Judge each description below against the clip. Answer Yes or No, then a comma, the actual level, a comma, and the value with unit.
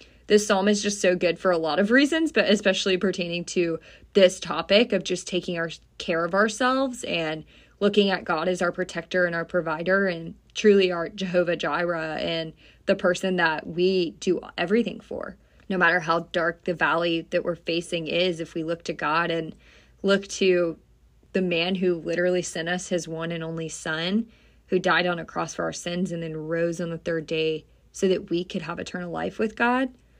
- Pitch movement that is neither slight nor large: No, narrow, 2.3 semitones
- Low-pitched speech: No, medium, 175 Hz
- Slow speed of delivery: No, average, 200 wpm